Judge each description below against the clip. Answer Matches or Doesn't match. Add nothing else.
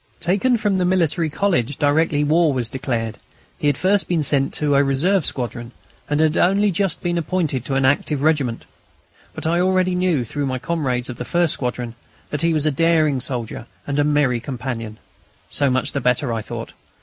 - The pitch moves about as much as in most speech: Matches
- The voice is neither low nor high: Matches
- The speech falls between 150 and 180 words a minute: Doesn't match